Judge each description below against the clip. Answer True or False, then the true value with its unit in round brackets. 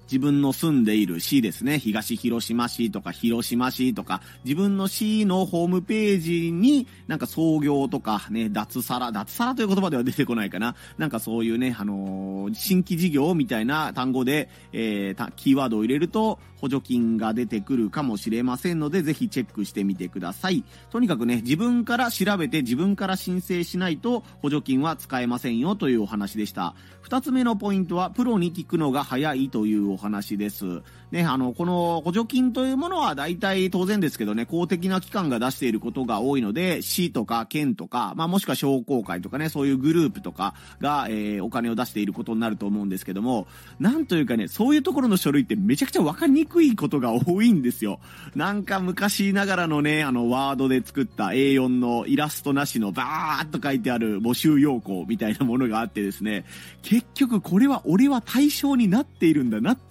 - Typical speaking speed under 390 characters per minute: False (400 characters per minute)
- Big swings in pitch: True (8.8 semitones)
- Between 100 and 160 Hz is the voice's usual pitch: True (140 Hz)